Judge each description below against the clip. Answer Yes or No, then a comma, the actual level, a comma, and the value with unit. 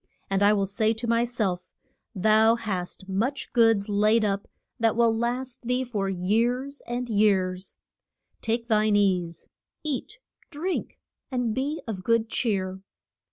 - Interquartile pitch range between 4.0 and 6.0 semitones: No, average, 3.3 semitones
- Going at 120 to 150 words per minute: Yes, average, 140 wpm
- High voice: Yes, high, 220 Hz